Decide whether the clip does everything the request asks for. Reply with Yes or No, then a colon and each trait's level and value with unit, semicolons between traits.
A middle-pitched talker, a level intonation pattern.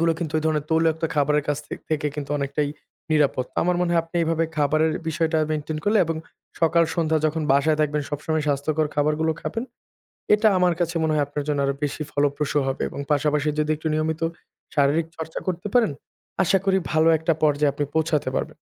Yes: medium, 155 Hz; narrow, 1.9 semitones